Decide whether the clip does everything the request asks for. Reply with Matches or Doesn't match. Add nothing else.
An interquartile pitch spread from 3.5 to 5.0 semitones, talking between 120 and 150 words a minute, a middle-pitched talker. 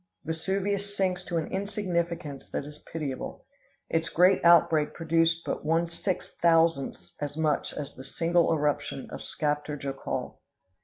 Doesn't match